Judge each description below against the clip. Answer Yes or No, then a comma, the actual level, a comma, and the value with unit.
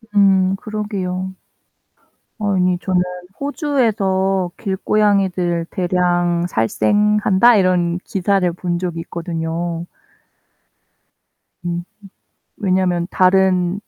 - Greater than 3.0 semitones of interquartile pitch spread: No, narrow, 2.2 semitones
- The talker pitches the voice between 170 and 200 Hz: Yes, medium, 185 Hz